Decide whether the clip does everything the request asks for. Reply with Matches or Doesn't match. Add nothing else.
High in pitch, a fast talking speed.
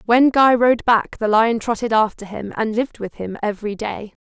Matches